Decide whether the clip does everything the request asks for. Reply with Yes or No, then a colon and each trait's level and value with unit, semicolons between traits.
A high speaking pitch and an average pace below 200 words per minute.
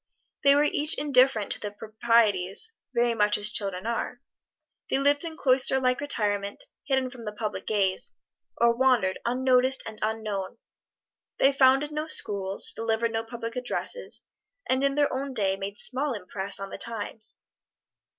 Yes: high, 235 Hz; average, 155 wpm